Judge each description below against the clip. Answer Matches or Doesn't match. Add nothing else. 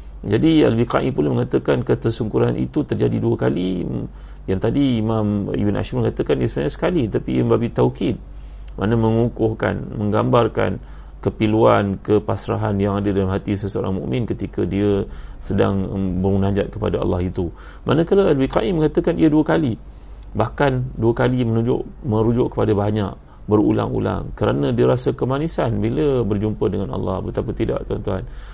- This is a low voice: Matches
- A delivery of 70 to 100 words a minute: Doesn't match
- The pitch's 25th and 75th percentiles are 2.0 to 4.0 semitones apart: Matches